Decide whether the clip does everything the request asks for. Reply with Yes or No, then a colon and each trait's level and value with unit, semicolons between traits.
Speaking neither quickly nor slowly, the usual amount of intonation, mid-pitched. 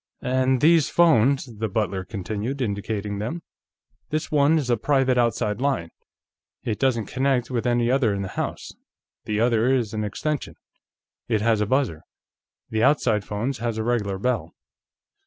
No: average, 155 wpm; average, 4.0 semitones; low, 120 Hz